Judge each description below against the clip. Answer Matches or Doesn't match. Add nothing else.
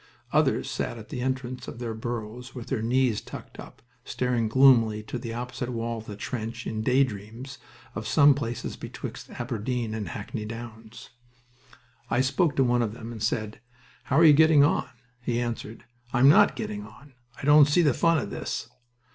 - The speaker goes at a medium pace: Matches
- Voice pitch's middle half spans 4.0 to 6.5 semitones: Doesn't match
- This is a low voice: Matches